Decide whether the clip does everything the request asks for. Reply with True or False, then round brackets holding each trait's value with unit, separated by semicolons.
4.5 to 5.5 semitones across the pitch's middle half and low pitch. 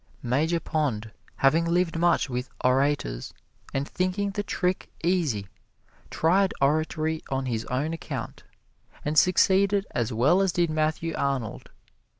False (4.9 semitones; 155 Hz)